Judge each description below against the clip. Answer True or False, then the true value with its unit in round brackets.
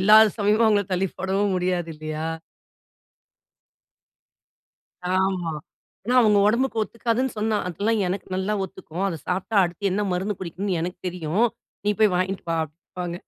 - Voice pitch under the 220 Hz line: True (190 Hz)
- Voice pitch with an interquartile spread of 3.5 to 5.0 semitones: False (3.0 semitones)